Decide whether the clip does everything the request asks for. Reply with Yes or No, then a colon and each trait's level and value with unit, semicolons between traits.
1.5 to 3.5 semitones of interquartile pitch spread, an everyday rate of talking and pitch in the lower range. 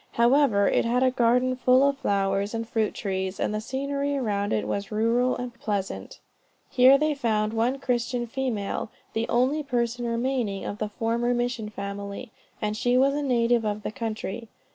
No: average, 3.1 semitones; average, 175 wpm; high, 235 Hz